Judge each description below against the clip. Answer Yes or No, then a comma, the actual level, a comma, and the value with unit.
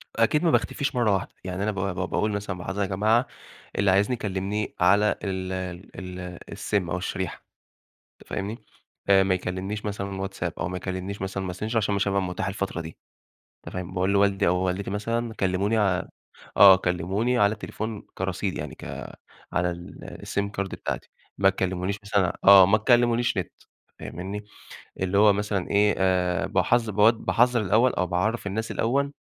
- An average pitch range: No, narrow, 2.2 semitones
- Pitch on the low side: Yes, low, 100 Hz